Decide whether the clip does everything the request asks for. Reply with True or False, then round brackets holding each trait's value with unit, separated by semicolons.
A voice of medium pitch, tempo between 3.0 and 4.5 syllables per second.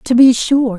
False (245 Hz; 4.4 syllables/s)